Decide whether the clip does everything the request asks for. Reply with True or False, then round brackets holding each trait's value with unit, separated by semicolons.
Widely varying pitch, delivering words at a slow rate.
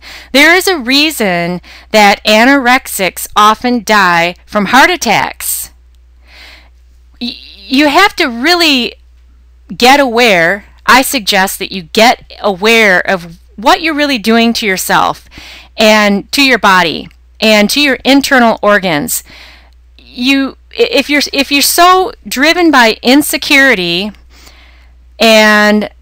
True (7.6 semitones; 115 wpm)